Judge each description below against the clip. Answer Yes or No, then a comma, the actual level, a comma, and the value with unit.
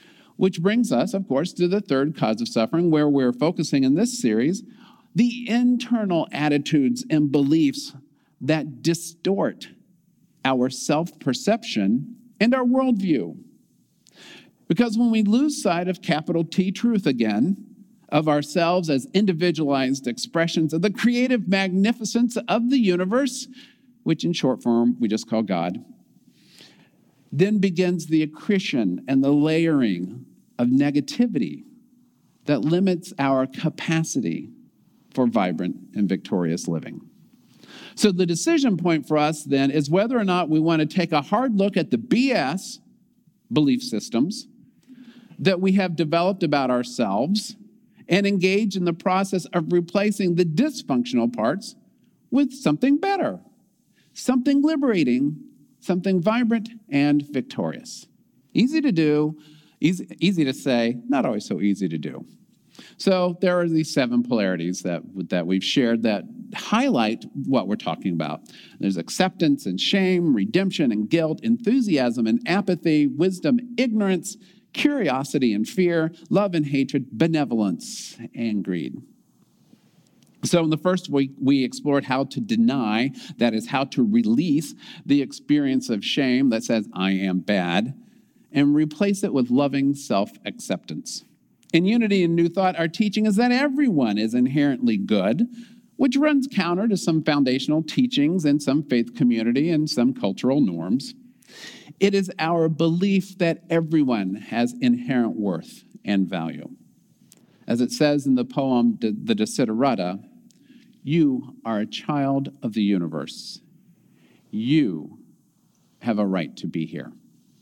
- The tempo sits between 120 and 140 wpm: Yes, slow, 135 wpm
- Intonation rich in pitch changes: Yes, wide, 8.3 semitones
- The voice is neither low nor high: Yes, medium, 175 Hz